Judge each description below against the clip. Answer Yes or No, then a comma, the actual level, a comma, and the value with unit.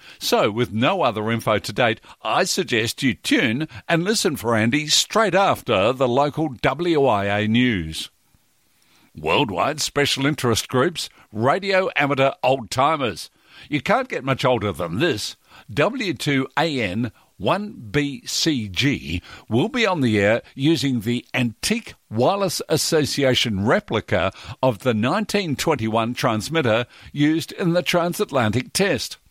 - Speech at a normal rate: No, slow, 115 wpm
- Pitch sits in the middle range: No, low, 130 Hz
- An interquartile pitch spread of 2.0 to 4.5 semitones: No, average, 4.9 semitones